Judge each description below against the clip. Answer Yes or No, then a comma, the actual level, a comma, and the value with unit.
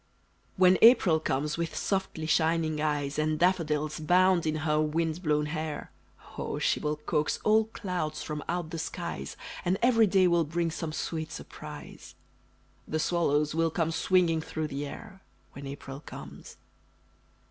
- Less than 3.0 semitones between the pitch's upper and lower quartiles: Yes, narrow, 2.5 semitones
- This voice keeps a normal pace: Yes, average, 150 wpm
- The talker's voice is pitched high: No, medium, 160 Hz